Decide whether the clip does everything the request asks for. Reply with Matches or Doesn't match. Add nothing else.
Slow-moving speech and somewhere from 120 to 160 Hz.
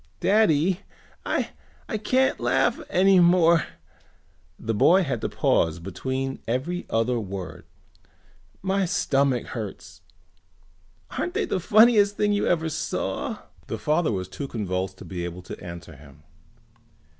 Matches